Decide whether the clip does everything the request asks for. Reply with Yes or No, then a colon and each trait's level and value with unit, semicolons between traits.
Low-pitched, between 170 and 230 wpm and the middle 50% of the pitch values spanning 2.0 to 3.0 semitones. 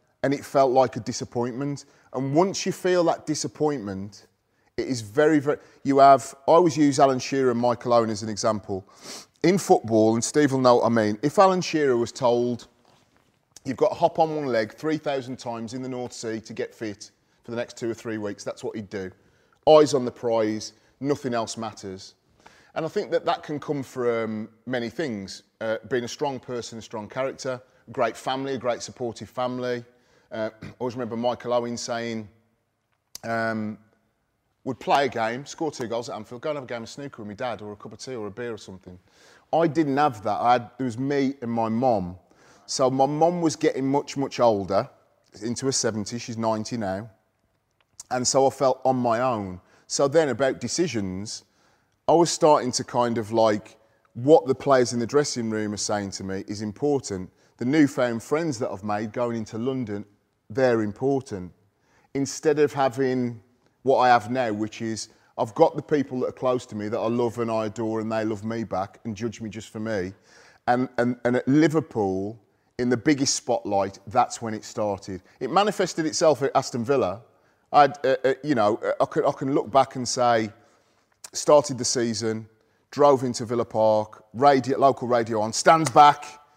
No: low, 120 Hz; average, 200 wpm; average, 3.7 semitones